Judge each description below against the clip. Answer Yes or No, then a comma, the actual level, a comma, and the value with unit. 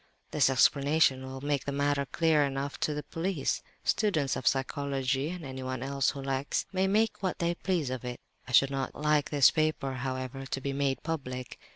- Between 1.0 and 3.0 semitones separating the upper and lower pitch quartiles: Yes, narrow, 2.5 semitones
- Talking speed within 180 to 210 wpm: Yes, average, 190 wpm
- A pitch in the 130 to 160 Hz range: Yes, medium, 140 Hz